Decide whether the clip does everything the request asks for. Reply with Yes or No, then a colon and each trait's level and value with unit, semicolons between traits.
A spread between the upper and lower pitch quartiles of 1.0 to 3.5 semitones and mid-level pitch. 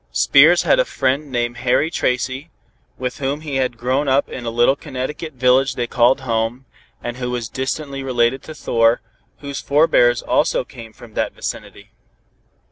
No: narrow, 2.4 semitones; low, 130 Hz